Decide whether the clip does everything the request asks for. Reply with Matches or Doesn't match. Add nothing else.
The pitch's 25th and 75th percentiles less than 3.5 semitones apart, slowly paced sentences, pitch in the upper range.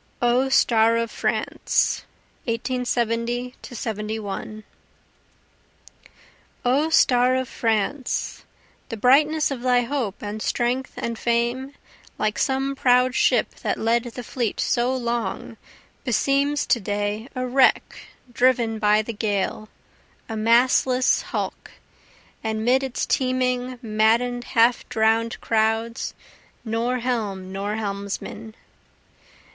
Matches